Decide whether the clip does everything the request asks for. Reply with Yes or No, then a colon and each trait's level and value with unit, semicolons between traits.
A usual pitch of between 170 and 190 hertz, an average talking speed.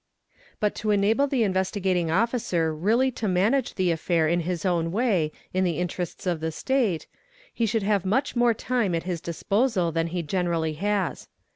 Yes: medium, 185 Hz; average, 180 wpm